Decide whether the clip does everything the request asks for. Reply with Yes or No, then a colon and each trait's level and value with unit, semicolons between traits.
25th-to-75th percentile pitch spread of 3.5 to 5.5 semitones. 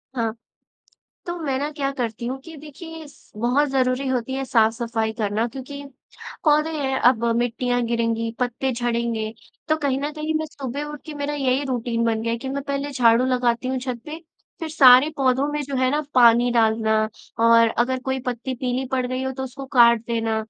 No: average, 3.1 semitones